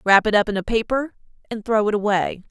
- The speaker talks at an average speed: No, fast, 240 wpm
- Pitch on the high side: Yes, high, 210 Hz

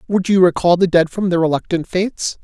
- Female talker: No, male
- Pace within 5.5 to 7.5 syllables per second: Yes, 5.8 syllables/s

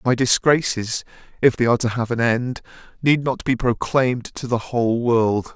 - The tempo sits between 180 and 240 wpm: Yes, average, 185 wpm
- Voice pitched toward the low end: Yes, low, 120 Hz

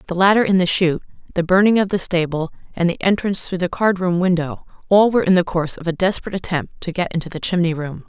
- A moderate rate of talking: No, fast, 240 wpm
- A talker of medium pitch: Yes, medium, 180 Hz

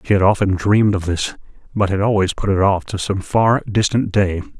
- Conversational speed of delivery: No, fast, 220 wpm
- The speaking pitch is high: No, low, 100 Hz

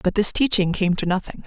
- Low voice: No, high, 195 Hz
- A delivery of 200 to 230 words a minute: No, fast, 245 wpm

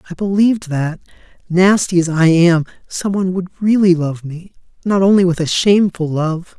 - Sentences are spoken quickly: No, average, 175 wpm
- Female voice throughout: No, male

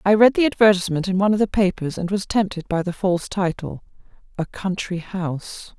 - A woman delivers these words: Yes, female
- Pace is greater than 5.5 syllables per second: Yes, 5.8 syllables/s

